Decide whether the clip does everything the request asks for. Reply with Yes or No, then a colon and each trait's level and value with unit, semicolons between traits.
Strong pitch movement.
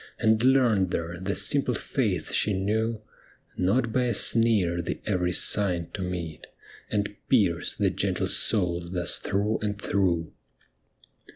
No: average, 3.9 semitones